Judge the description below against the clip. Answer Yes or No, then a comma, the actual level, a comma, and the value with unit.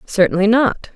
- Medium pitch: No, high, 210 Hz